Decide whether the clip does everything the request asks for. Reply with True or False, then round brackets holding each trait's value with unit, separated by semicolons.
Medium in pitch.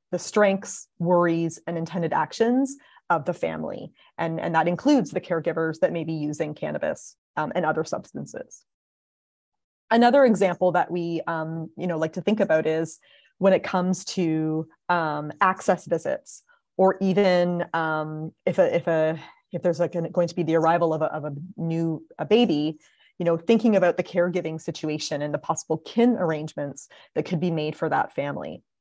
True (170 Hz)